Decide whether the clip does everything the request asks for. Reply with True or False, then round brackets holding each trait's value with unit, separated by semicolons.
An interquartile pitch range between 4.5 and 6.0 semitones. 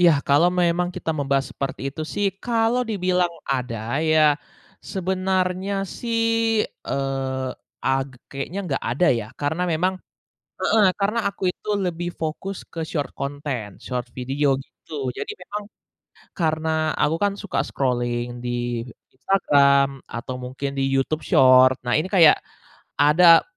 True (5.2 semitones)